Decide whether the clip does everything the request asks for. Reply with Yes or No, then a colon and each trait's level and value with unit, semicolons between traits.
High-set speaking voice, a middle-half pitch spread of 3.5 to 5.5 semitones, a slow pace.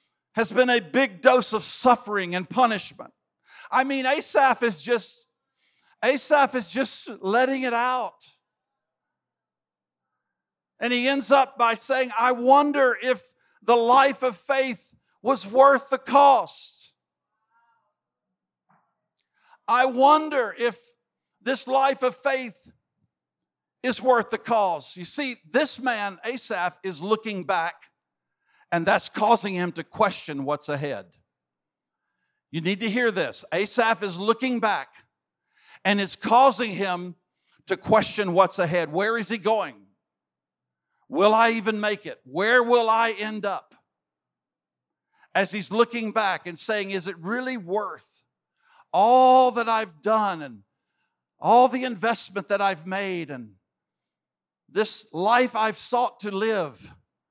Yes: high, 230 Hz; average, 4.4 semitones; slow, 130 wpm